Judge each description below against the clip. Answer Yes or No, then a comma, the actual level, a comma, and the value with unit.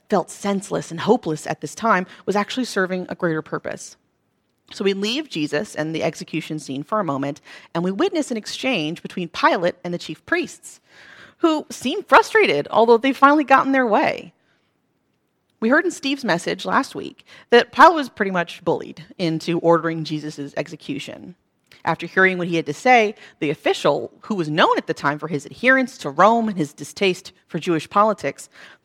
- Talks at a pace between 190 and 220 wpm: No, average, 180 wpm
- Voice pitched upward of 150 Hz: Yes, high, 190 Hz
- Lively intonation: Yes, wide, 7.3 semitones